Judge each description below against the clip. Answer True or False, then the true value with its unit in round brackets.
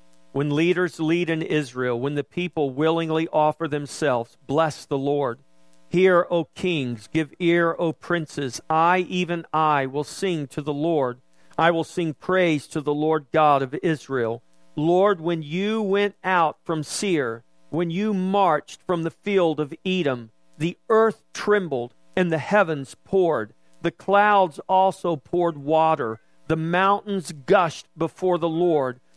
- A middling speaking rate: True (150 wpm)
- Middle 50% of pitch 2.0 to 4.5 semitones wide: True (3.8 semitones)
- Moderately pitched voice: True (160 Hz)